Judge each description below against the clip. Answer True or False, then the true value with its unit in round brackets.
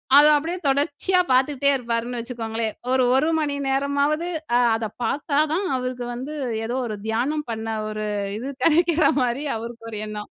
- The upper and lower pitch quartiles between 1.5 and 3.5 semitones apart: False (4.1 semitones)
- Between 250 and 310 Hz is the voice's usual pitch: True (260 Hz)